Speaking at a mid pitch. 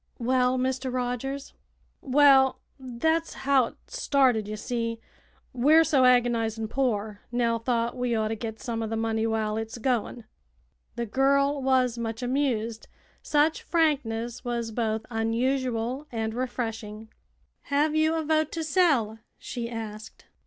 No: high, 245 Hz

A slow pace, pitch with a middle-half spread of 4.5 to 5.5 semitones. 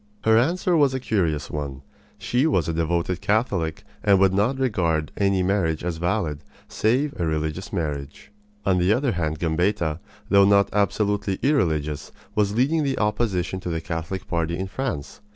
No: average, 165 wpm; average, 4.9 semitones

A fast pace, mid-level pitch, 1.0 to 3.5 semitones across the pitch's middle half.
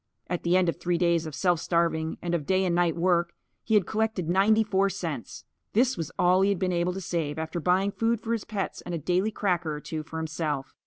Yes: fast, 245 wpm; medium, 175 Hz; average, 2.8 semitones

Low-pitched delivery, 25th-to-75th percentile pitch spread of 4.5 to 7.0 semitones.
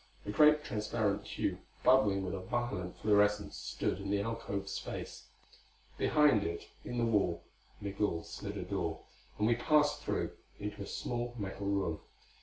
No: low, 105 Hz; average, 3.5 semitones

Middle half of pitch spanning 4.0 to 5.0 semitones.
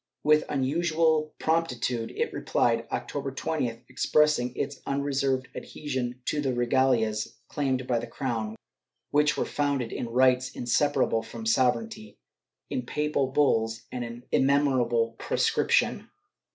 No: average, 3.5 semitones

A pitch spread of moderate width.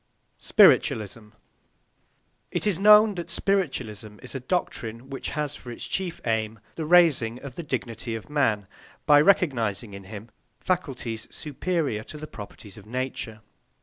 No: wide, 6.6 semitones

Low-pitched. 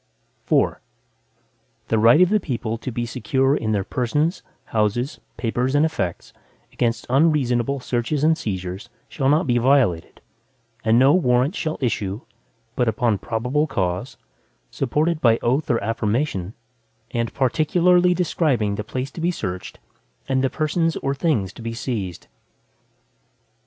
Yes: low, 125 Hz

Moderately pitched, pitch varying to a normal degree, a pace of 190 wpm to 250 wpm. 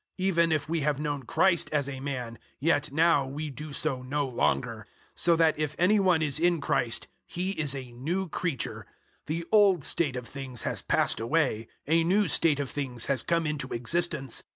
Yes: medium, 150 Hz; average, 4.0 semitones; average, 195 wpm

